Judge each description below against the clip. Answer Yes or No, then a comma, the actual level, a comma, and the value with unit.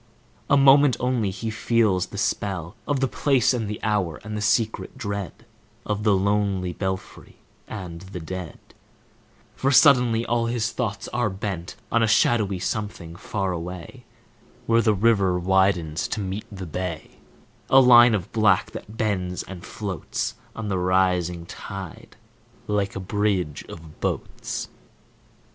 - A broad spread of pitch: No, average, 3.5 semitones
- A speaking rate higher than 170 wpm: No, average, 145 wpm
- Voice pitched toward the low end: Yes, low, 100 Hz